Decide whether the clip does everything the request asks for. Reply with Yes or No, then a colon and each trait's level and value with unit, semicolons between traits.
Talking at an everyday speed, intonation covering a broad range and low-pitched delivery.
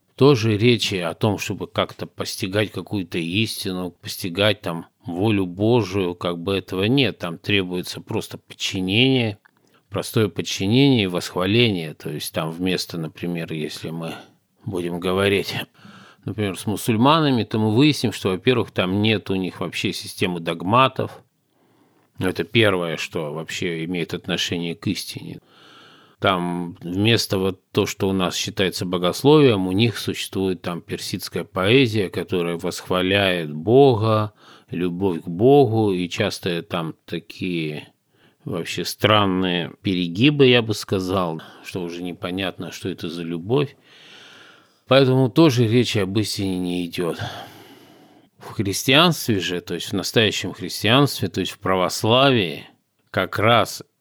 No: average, 130 wpm; average, 4.0 semitones; very low, 95 Hz